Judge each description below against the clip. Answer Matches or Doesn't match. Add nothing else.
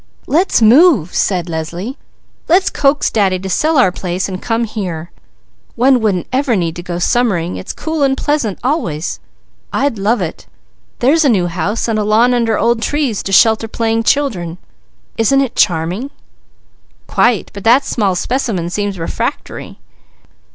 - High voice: Matches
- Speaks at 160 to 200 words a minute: Doesn't match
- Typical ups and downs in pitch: Doesn't match